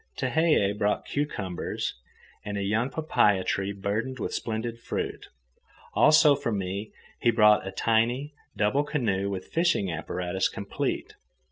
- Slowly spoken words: Yes, slow, 130 wpm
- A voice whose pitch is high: No, low, 105 Hz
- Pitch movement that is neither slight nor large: Yes, average, 5.0 semitones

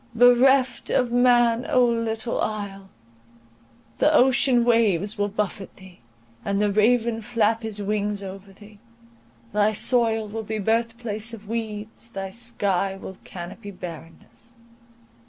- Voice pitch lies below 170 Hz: No, high, 220 Hz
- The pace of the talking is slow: Yes, slow, 130 wpm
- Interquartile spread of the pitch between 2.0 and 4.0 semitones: Yes, average, 2.7 semitones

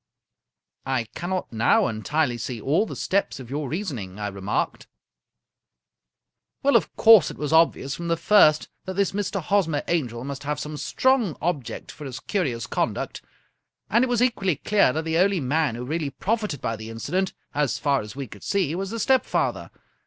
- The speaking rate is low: No, average, 190 wpm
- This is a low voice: No, medium, 155 Hz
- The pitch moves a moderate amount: No, wide, 7.2 semitones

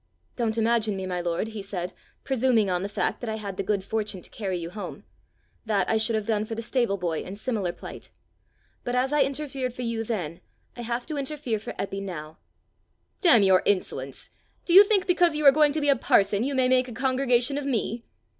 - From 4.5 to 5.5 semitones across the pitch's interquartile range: Yes, average, 4.8 semitones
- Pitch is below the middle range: No, high, 225 Hz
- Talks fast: Yes, fast, 220 wpm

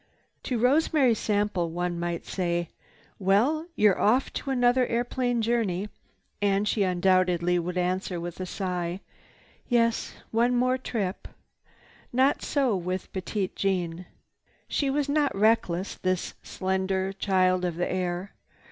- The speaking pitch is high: Yes, high, 195 Hz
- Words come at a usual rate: No, slow, 125 wpm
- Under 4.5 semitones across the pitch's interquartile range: No, average, 5.0 semitones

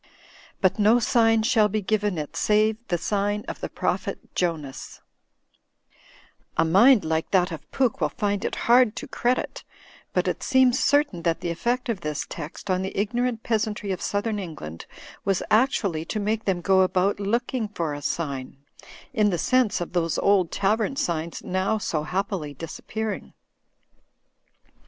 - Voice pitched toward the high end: Yes, high, 200 Hz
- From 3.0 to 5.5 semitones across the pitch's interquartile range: Yes, average, 4.5 semitones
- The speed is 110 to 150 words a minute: No, average, 160 wpm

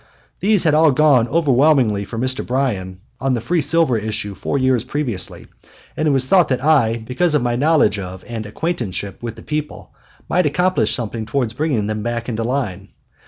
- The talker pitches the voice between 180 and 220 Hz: No, low, 125 Hz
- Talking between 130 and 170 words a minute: No, average, 185 wpm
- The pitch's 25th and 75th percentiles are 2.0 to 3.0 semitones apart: No, wide, 5.4 semitones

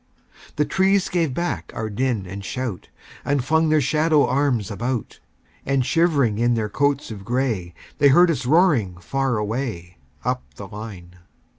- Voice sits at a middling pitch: No, low, 125 Hz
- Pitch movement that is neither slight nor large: No, wide, 5.9 semitones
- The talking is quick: No, average, 155 wpm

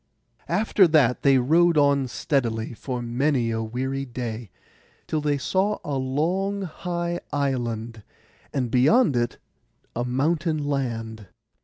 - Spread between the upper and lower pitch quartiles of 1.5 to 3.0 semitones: No, average, 4.7 semitones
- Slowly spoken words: Yes, slow, 125 wpm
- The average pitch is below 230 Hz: Yes, low, 135 Hz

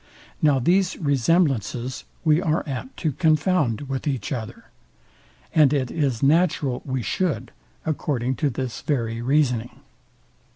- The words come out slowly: Yes, slow, 125 wpm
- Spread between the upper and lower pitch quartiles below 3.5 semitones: No, average, 3.8 semitones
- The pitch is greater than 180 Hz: No, medium, 140 Hz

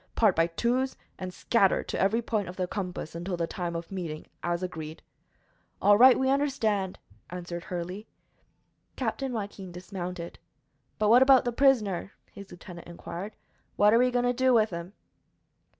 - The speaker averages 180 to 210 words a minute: No, average, 165 wpm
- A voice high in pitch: Yes, high, 195 Hz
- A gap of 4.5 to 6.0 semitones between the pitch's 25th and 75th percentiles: Yes, average, 5.2 semitones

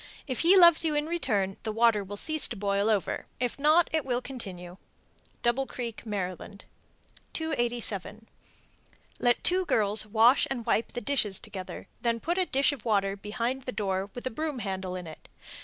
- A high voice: Yes, high, 230 Hz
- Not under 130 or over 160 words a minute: No, average, 175 wpm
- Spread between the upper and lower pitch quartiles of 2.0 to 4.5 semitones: No, average, 5.2 semitones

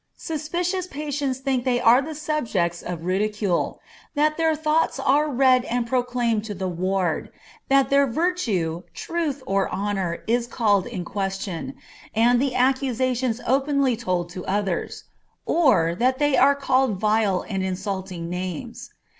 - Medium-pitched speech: No, high, 240 Hz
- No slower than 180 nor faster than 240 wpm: No, average, 145 wpm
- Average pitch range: No, wide, 6.2 semitones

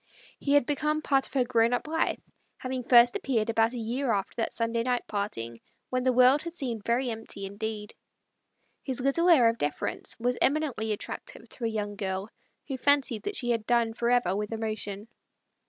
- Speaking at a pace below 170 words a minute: No, average, 190 wpm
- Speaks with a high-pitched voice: Yes, high, 235 Hz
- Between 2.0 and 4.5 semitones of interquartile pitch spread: Yes, average, 3.1 semitones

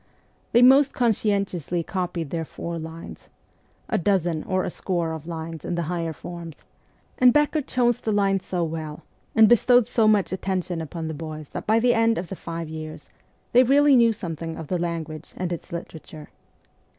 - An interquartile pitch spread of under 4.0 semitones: No, average, 5.1 semitones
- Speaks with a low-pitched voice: No, medium, 175 Hz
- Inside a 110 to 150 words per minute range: No, average, 180 wpm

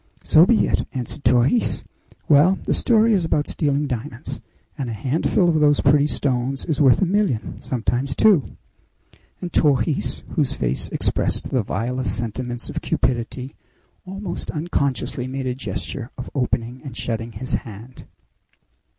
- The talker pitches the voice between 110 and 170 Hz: Yes, low, 135 Hz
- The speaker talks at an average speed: Yes, average, 145 wpm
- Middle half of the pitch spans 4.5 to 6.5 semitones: No, average, 3.8 semitones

